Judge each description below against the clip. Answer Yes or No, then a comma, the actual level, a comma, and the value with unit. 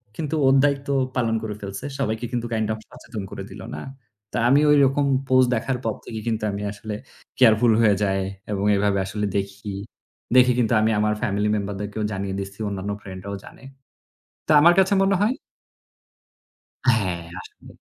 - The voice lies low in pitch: Yes, low, 110 Hz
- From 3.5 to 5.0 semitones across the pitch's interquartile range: Yes, average, 4.1 semitones